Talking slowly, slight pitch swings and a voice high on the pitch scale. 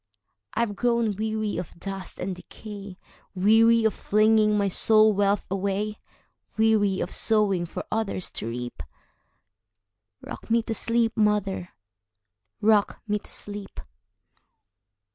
No: slow, 105 wpm; average, 3.5 semitones; high, 205 Hz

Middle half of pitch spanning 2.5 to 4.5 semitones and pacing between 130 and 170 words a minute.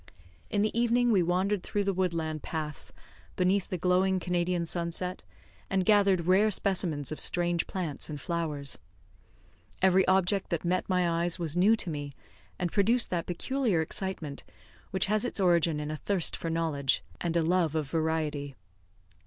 Yes: average, 2.9 semitones; average, 160 wpm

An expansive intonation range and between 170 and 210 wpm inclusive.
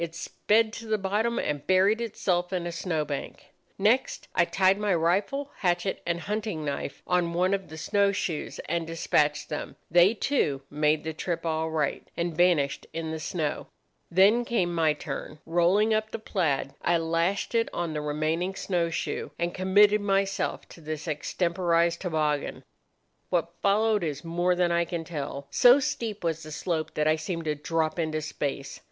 No: average, 3.8 semitones; average, 175 wpm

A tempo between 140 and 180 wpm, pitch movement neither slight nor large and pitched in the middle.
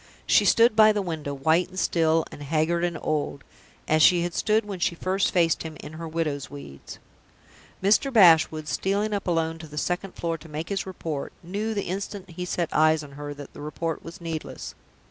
No: fast, 205 wpm; average, 3.3 semitones; medium, 165 Hz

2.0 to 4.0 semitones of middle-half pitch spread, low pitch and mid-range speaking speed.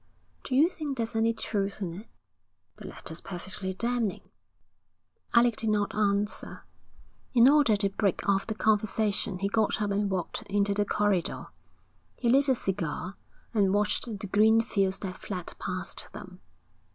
No: narrow, 2.4 semitones; high, 205 Hz; average, 155 wpm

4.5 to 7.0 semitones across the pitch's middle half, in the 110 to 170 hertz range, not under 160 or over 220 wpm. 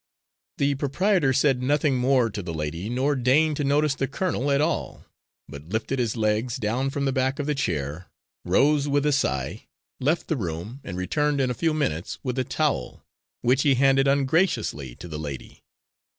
Yes: average, 5.1 semitones; low, 135 Hz; average, 185 wpm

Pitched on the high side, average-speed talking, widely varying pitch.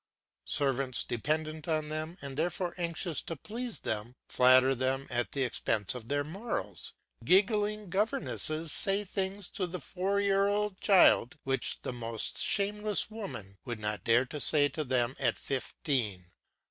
No: medium, 155 Hz; average, 150 wpm; wide, 7.3 semitones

